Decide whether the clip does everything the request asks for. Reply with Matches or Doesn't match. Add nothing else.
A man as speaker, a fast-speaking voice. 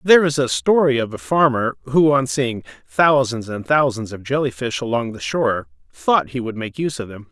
Matches